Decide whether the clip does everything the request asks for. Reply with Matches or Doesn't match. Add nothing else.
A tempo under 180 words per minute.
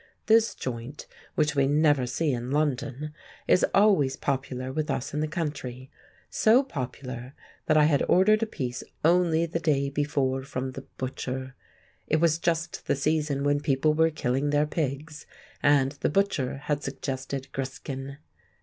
Matches